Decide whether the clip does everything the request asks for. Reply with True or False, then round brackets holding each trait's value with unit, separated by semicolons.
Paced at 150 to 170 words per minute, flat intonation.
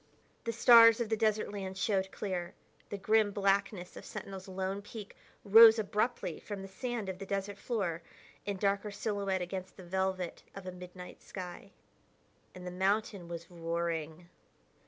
True (155 wpm; 2.3 semitones)